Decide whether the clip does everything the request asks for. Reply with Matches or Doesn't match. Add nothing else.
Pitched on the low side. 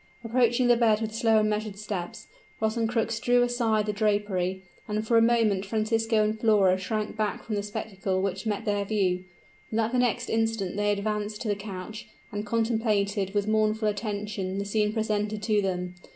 Doesn't match